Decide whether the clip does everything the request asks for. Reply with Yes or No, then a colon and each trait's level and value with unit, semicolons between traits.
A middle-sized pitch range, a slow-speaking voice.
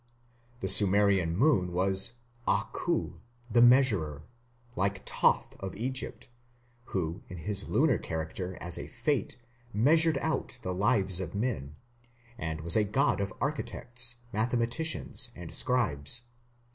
No: wide, 5.7 semitones; slow, 120 wpm